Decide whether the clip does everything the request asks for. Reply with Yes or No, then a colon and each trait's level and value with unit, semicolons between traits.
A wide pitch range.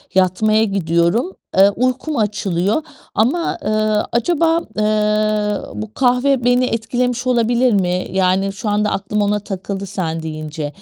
No: average, 4.3 semitones